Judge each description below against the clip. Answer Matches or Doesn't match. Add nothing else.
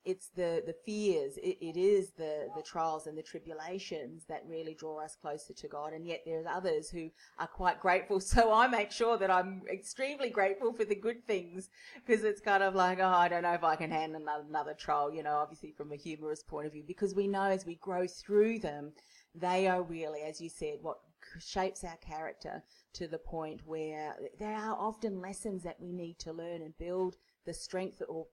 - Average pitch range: Matches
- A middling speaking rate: Doesn't match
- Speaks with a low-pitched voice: Doesn't match